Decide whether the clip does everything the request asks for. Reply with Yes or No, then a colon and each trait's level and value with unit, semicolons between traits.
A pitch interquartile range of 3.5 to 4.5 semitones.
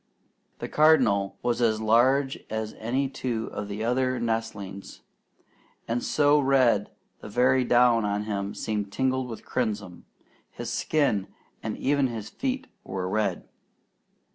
Yes: average, 3.8 semitones